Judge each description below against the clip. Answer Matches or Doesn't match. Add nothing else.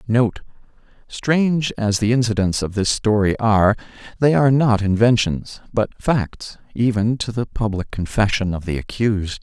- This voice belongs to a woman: Doesn't match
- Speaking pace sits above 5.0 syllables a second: Doesn't match